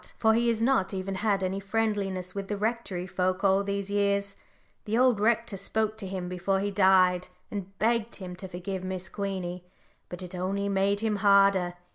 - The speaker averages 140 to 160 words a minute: No, average, 185 wpm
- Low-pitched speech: No, high, 195 Hz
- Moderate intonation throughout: No, narrow, 1.9 semitones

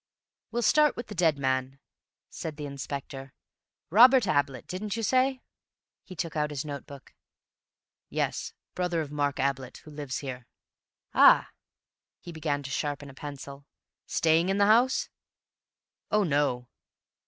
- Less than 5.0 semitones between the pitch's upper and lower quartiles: No, wide, 5.4 semitones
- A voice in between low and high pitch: Yes, medium, 150 Hz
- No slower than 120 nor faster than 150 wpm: Yes, average, 140 wpm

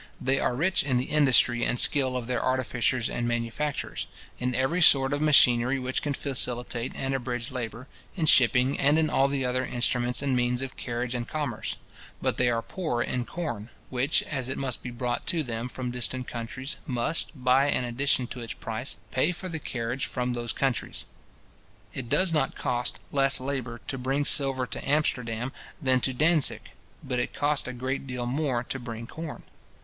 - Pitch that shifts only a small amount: Yes, narrow, 2.3 semitones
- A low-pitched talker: Yes, low, 130 Hz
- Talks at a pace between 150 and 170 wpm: No, average, 185 wpm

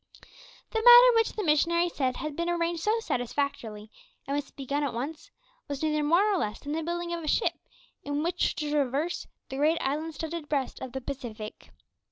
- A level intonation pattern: No, average, 3.7 semitones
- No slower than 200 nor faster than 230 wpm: Yes, fast, 205 wpm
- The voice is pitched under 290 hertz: No, very high, 300 Hz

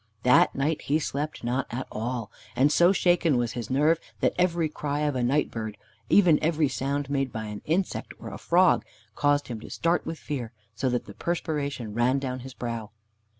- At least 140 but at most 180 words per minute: No, average, 195 wpm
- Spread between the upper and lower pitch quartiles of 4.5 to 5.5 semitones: No, average, 4.0 semitones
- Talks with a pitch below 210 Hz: Yes, medium, 140 Hz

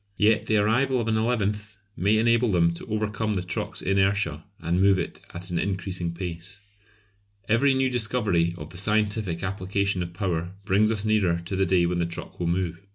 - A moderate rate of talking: Yes, average, 190 wpm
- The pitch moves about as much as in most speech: Yes, average, 3.6 semitones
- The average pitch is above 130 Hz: No, low, 100 Hz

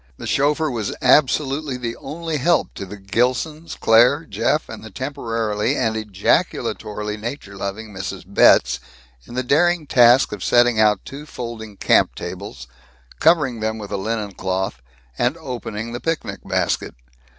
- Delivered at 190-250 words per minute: No, average, 150 wpm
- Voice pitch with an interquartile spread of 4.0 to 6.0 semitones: Yes, average, 5.0 semitones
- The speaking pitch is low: Yes, low, 115 Hz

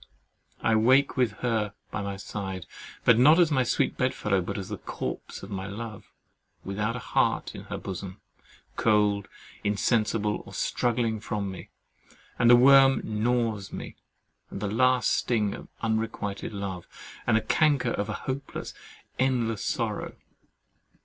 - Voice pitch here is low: Yes, low, 110 Hz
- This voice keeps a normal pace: Yes, average, 145 wpm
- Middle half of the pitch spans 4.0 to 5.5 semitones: No, average, 3.3 semitones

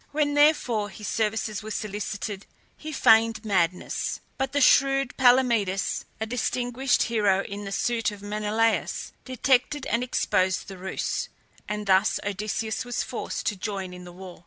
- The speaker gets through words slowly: No, average, 150 wpm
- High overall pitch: Yes, high, 215 Hz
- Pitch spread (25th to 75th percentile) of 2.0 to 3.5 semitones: No, average, 3.9 semitones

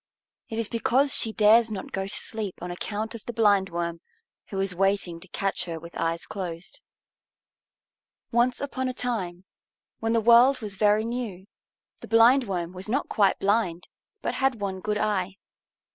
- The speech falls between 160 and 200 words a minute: Yes, average, 170 wpm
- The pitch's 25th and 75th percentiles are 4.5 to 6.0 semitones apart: No, average, 3.8 semitones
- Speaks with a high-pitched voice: Yes, high, 210 Hz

